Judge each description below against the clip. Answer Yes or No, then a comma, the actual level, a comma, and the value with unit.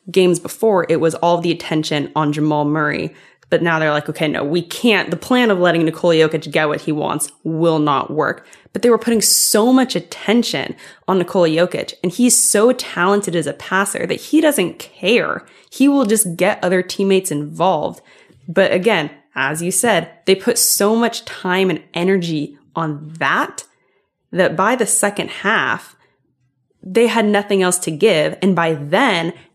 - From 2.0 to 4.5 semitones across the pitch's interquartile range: No, average, 5.1 semitones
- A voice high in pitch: No, medium, 175 Hz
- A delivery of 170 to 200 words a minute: Yes, average, 175 wpm